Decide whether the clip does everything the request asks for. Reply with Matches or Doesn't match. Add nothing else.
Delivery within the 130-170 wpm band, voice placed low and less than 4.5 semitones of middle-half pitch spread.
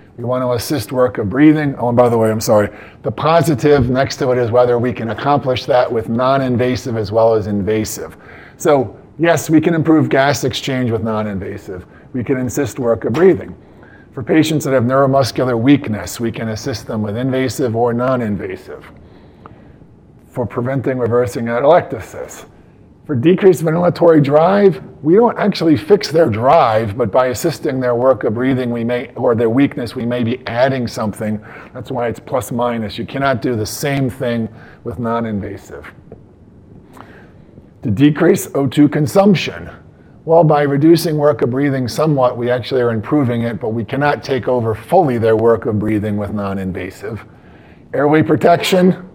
Matches